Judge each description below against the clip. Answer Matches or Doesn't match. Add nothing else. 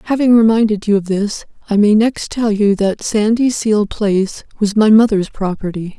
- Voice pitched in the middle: Doesn't match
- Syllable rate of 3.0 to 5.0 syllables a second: Matches